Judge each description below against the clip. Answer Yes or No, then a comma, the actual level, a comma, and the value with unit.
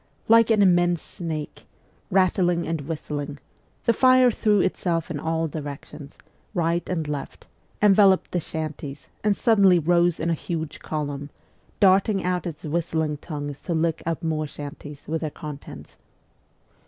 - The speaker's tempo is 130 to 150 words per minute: Yes, average, 140 wpm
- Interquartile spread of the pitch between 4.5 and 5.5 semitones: No, average, 3.3 semitones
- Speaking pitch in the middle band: Yes, medium, 165 Hz